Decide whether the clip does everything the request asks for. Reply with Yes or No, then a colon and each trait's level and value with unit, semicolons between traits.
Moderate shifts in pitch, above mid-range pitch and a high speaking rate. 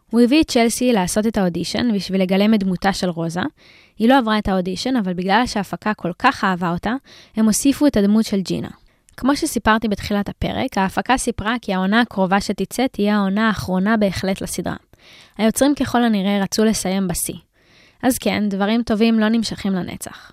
Yes: average, 3.5 semitones; high, 210 Hz; fast, 175 wpm